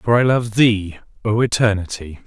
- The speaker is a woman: No, male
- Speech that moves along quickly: No, average, 160 wpm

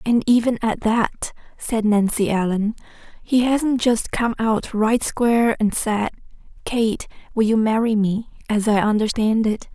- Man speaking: No, female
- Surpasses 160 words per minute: No, average, 155 wpm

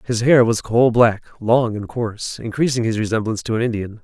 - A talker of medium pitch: No, low, 115 Hz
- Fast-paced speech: Yes, fast, 210 wpm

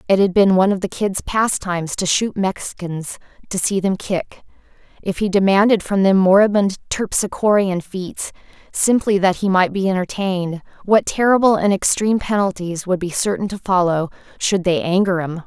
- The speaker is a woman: Yes, female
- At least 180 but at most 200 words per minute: No, average, 165 wpm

